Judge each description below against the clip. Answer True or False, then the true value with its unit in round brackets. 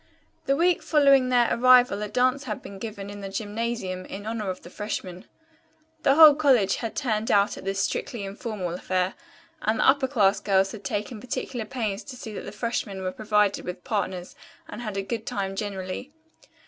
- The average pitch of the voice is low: False (210 Hz)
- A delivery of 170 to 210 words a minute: True (190 wpm)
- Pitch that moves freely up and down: False (4.1 semitones)